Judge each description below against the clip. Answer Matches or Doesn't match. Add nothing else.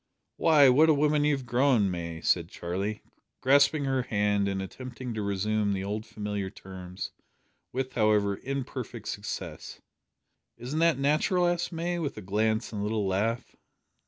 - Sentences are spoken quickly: Doesn't match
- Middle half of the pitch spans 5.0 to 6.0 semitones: Matches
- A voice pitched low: Matches